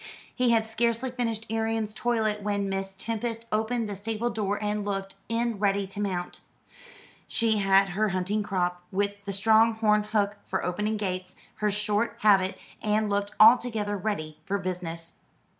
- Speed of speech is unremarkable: Yes, average, 160 wpm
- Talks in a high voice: Yes, high, 210 Hz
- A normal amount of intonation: No, narrow, 2.3 semitones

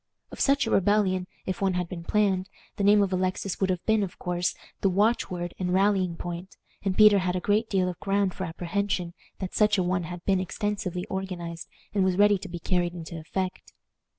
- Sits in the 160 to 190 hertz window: Yes, medium, 185 Hz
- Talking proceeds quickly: Yes, fast, 210 wpm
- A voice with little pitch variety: Yes, narrow, 2.2 semitones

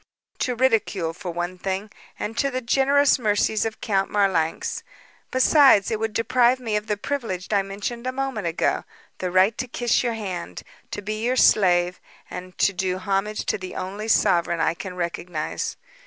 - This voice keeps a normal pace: Yes, average, 175 wpm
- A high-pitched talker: Yes, high, 205 Hz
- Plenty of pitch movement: No, average, 4.3 semitones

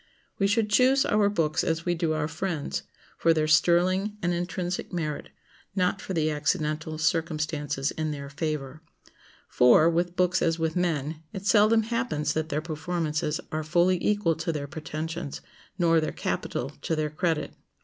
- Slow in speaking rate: No, average, 160 wpm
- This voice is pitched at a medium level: Yes, medium, 160 Hz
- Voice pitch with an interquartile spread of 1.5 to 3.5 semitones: Yes, average, 2.8 semitones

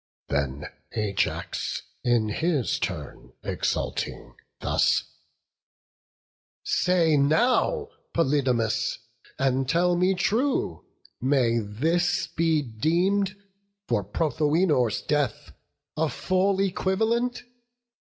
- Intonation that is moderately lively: No, wide, 7.3 semitones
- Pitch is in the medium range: Yes, medium, 155 Hz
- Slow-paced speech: Yes, slow, 80 wpm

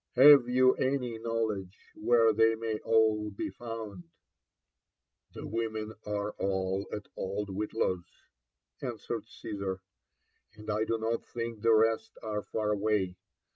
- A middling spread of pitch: No, narrow, 1.8 semitones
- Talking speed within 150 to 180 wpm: No, average, 140 wpm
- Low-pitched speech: Yes, low, 110 Hz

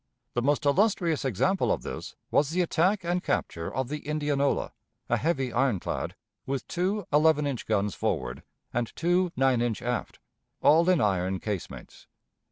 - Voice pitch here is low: No, medium, 145 Hz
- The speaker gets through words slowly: No, average, 155 wpm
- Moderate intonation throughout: No, wide, 6.1 semitones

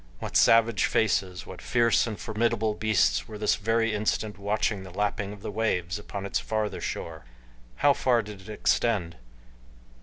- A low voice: Yes, low, 105 Hz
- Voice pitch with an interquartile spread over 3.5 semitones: No, narrow, 2.4 semitones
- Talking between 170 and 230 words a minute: No, average, 160 wpm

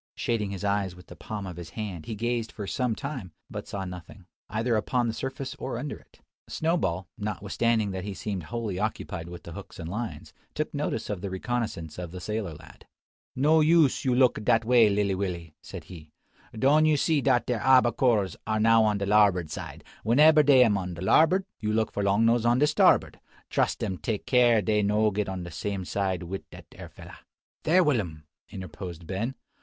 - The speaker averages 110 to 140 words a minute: No, fast, 205 wpm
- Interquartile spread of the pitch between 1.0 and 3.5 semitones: No, average, 4.4 semitones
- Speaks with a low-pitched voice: Yes, low, 105 Hz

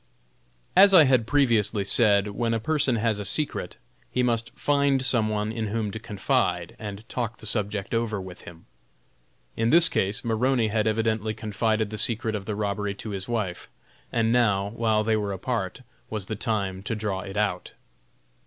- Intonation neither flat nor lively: No, narrow, 2.3 semitones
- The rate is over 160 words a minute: Yes, average, 180 wpm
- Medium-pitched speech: No, low, 110 Hz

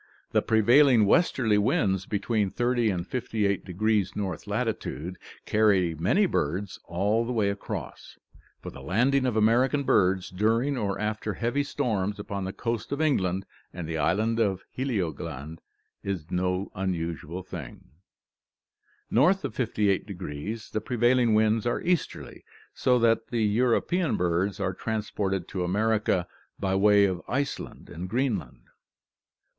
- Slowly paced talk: Yes, slow, 130 wpm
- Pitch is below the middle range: Yes, low, 105 Hz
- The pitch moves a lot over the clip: No, average, 4.0 semitones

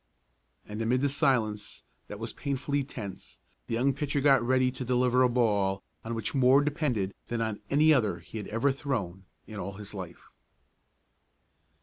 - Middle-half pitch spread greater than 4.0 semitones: Yes, average, 4.5 semitones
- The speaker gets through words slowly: No, average, 165 wpm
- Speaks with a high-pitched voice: No, low, 120 Hz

